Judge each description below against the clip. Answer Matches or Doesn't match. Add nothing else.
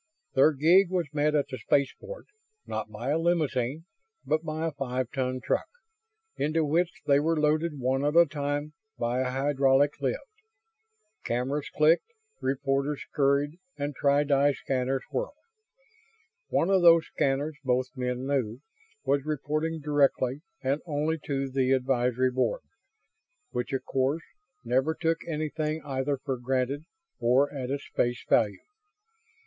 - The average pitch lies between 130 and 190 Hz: Matches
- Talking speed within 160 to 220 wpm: Doesn't match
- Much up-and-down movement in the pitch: Doesn't match